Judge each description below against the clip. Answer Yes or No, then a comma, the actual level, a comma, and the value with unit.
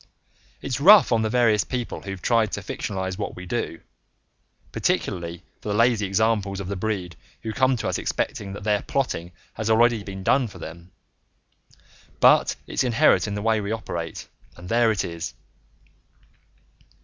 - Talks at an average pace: Yes, average, 165 wpm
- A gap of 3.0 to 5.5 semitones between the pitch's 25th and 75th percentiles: Yes, average, 3.4 semitones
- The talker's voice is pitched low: Yes, low, 105 Hz